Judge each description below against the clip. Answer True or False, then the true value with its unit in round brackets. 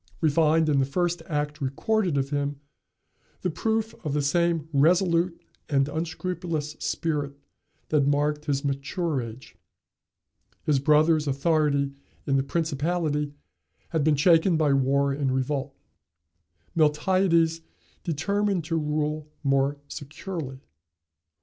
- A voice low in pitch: False (150 Hz)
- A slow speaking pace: True (120 wpm)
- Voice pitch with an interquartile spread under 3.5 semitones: True (3.0 semitones)